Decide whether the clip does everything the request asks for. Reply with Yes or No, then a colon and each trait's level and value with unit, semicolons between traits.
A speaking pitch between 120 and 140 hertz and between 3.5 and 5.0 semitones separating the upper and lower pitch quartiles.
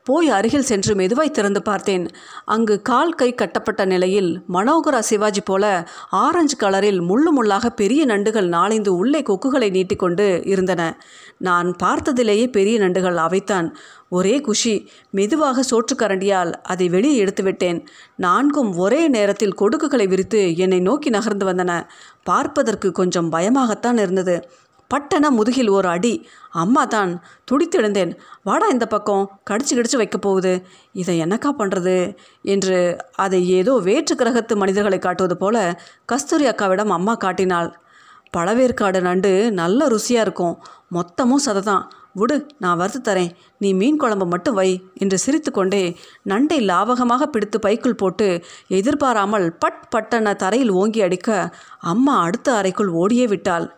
No: high, 205 Hz; average, 4.6 semitones